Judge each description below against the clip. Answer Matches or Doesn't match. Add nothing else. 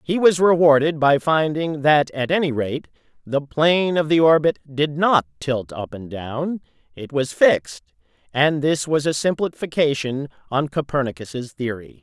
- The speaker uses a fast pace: Doesn't match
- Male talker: Matches